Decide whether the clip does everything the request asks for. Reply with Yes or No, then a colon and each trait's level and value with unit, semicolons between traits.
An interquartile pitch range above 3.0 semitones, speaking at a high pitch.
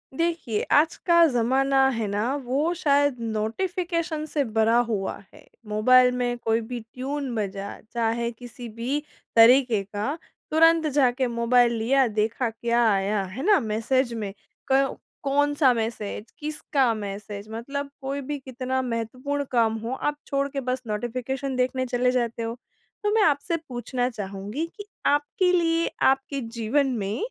Yes: average, 3.8 semitones; very high, 250 Hz